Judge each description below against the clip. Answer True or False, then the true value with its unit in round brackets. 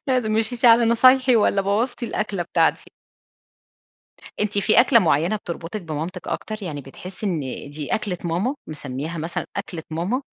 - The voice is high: True (200 Hz)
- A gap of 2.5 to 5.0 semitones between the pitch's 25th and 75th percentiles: False (5.5 semitones)